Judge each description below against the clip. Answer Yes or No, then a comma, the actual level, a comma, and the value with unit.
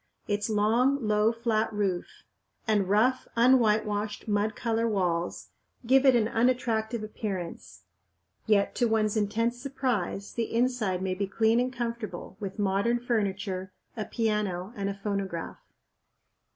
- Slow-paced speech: Yes, slow, 130 wpm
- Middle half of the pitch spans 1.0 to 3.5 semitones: Yes, average, 2.8 semitones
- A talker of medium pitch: No, high, 215 Hz